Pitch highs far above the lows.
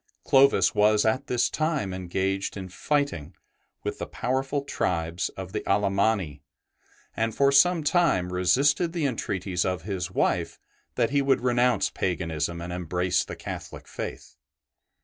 Yes: wide, 7.1 semitones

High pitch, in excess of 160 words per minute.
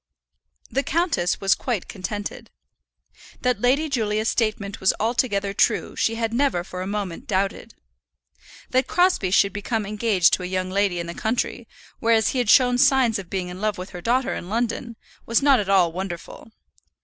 Yes: high, 210 Hz; average, 175 wpm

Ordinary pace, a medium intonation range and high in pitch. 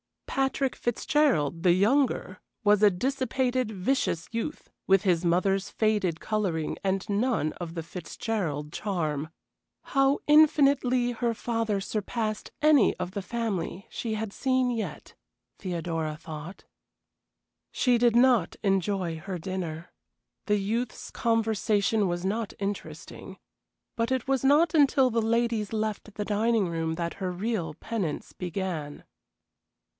No: slow, 125 wpm; average, 5.0 semitones; high, 210 Hz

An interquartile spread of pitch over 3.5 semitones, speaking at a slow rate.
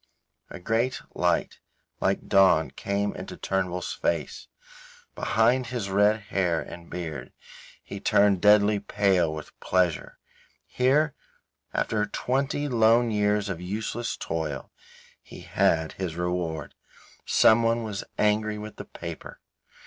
Yes: average, 3.9 semitones; slow, 120 wpm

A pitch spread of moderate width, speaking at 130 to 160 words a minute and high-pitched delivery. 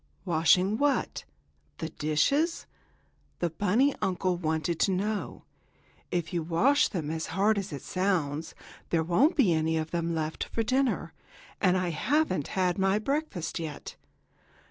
No: average, 4.7 semitones; average, 145 wpm; medium, 180 Hz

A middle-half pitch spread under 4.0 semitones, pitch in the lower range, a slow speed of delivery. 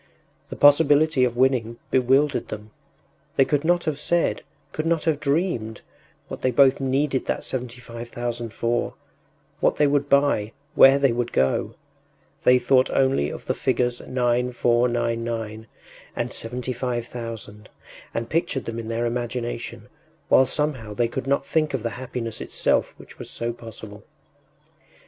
No: average, 2.9 semitones; low, 125 Hz; average, 145 wpm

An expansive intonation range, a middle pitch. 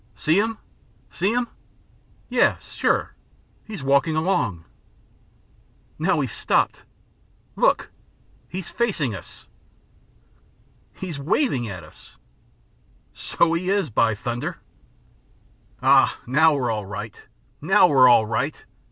Yes: wide, 8.3 semitones; medium, 145 Hz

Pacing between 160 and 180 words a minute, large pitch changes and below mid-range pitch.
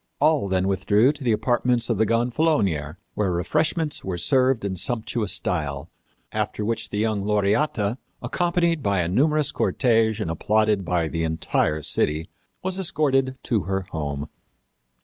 No: average, 150 wpm; wide, 6.1 semitones; low, 110 Hz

